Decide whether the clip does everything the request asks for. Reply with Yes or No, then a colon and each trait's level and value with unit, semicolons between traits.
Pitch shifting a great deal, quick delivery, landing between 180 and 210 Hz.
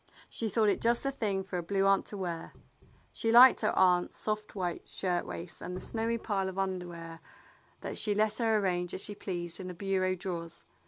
No: average, 3.1 semitones; fast, 210 wpm; high, 190 Hz